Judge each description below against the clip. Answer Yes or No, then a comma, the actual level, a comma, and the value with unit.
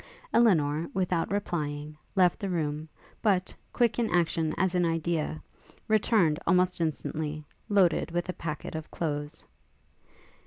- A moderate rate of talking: No, slow, 125 wpm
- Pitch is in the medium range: Yes, medium, 170 Hz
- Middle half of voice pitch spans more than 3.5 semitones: No, average, 3.1 semitones